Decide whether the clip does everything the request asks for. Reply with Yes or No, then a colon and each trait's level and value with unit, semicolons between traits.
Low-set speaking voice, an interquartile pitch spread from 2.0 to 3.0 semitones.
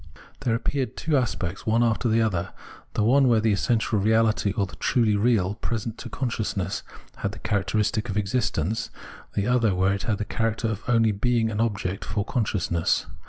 Yes: low, 110 Hz; narrow, 2.6 semitones